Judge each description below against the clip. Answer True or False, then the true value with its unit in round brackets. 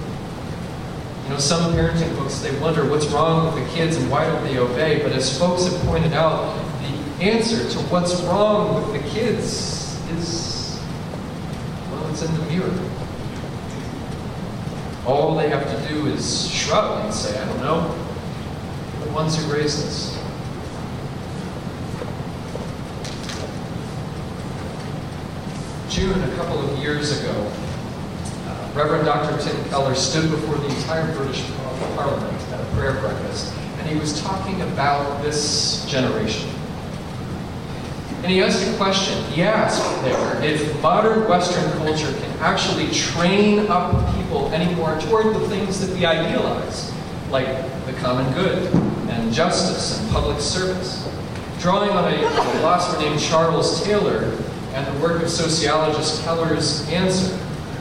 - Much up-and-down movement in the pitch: False (3.1 semitones)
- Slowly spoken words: True (130 wpm)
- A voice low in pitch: False (155 Hz)